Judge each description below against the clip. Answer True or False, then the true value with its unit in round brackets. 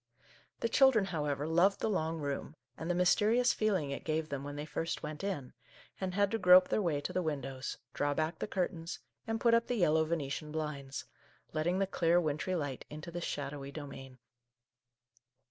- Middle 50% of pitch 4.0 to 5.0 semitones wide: True (4.3 semitones)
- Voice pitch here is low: False (160 Hz)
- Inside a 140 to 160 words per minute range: False (190 wpm)